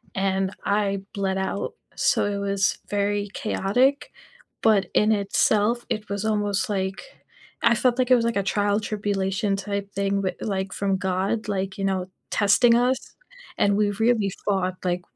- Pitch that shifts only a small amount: Yes, narrow, 1.7 semitones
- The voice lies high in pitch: Yes, high, 200 Hz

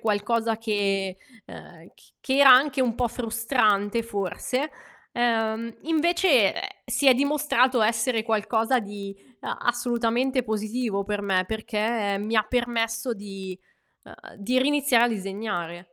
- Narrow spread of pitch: No, average, 3.4 semitones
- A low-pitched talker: No, high, 225 Hz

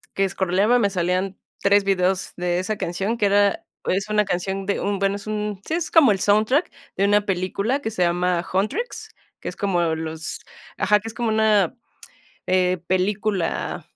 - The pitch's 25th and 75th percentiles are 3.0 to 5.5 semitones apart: No, narrow, 2.5 semitones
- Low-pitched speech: No, high, 195 Hz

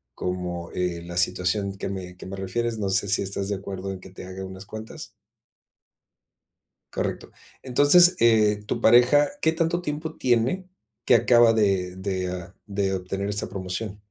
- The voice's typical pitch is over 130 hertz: No, low, 100 Hz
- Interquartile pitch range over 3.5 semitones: Yes, average, 4.1 semitones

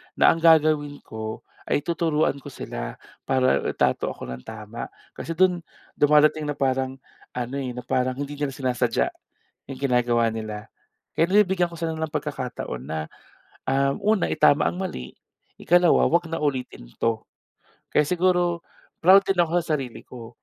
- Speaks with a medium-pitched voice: Yes, medium, 145 Hz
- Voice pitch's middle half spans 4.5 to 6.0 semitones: Yes, average, 5.0 semitones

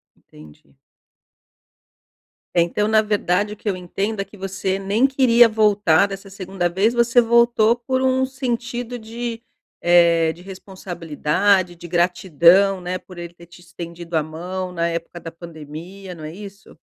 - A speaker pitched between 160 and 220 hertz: Yes, high, 190 Hz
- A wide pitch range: No, average, 4.1 semitones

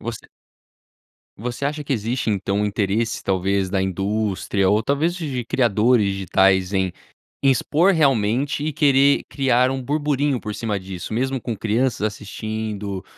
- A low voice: Yes, low, 110 Hz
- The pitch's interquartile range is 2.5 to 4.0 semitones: No, average, 5.2 semitones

